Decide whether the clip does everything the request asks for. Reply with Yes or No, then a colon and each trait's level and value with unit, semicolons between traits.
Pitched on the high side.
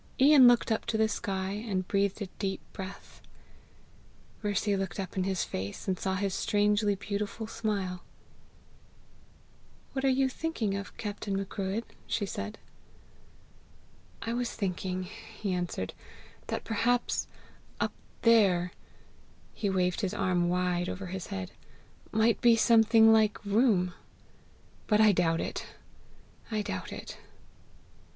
Yes: high, 200 Hz